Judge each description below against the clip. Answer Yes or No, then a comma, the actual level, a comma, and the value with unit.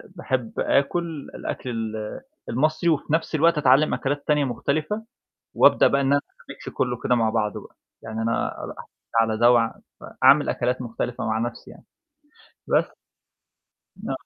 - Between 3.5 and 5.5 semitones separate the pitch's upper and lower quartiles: Yes, average, 4.7 semitones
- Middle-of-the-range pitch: No, low, 125 Hz